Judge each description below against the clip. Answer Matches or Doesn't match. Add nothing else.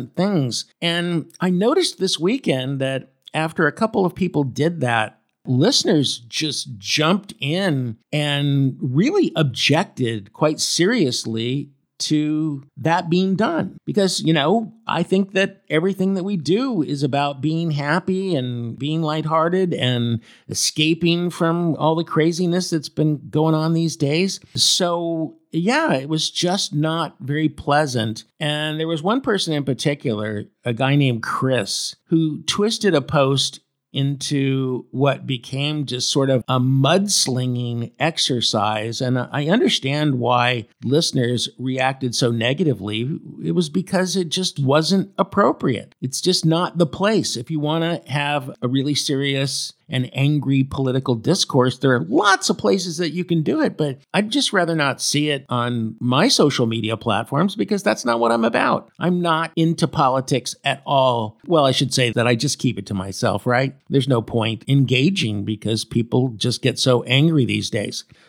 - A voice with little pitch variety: Doesn't match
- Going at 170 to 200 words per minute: Doesn't match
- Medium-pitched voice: Matches